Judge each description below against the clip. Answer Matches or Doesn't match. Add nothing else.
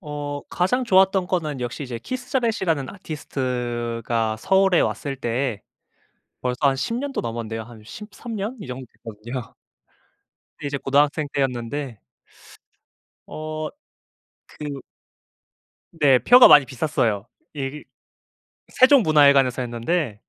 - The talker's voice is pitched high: Doesn't match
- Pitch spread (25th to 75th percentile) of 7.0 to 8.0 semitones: Doesn't match